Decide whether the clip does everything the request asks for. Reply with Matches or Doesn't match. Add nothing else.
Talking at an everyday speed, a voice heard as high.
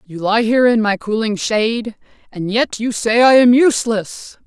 Matches